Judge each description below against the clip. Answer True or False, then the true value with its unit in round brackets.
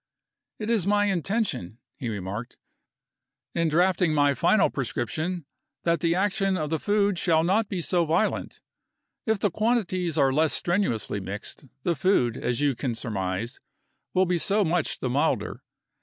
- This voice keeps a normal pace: True (155 wpm)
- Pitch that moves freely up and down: True (6.4 semitones)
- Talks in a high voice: False (170 Hz)